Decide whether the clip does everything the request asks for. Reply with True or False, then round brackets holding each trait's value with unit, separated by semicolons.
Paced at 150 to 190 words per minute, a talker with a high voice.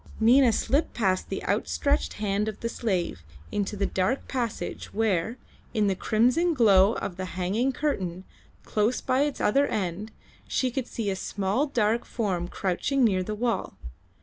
True (160 wpm; 215 Hz)